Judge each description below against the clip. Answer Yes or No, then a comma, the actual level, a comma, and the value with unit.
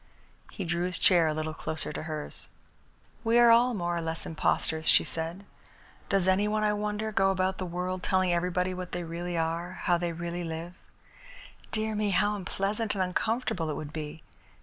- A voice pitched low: No, medium, 180 Hz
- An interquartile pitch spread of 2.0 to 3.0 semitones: No, average, 3.5 semitones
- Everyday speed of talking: Yes, average, 190 wpm